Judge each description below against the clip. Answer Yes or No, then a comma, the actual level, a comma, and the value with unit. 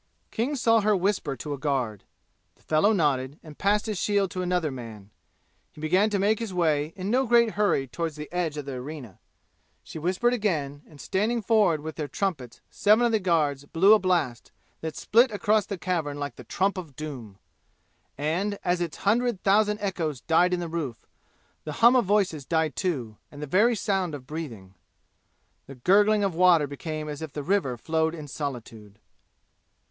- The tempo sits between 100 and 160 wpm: No, average, 185 wpm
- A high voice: No, medium, 165 Hz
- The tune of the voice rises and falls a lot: Yes, wide, 5.9 semitones